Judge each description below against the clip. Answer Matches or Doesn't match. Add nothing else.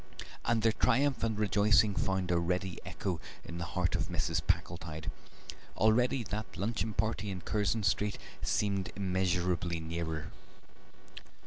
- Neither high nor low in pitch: Doesn't match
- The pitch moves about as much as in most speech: Matches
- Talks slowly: Matches